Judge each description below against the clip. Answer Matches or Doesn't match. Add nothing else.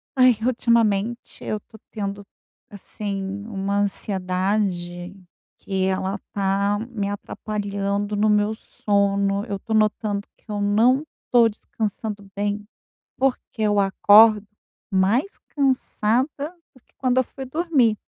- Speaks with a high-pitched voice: Matches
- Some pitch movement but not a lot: Doesn't match